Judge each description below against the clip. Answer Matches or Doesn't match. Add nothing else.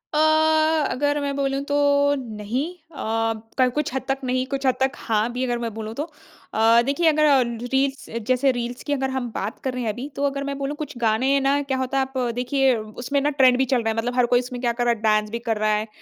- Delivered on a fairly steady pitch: Doesn't match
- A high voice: Matches